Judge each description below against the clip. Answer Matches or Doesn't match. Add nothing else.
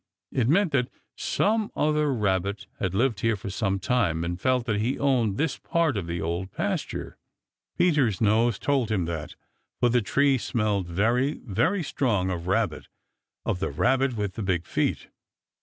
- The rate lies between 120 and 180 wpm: Matches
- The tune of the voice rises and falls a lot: Matches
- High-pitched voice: Doesn't match